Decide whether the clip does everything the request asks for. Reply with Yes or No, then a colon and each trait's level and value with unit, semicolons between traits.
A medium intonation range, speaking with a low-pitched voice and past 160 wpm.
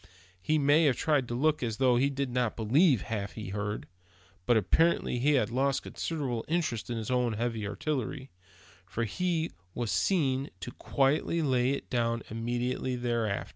Yes: average, 3.5 semitones; low, 125 Hz; average, 170 wpm